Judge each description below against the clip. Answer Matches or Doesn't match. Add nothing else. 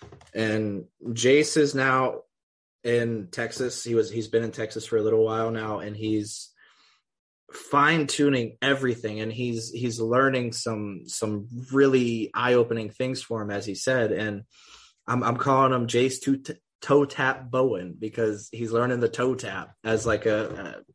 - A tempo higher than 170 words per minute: Doesn't match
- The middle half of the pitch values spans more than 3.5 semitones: Doesn't match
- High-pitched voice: Doesn't match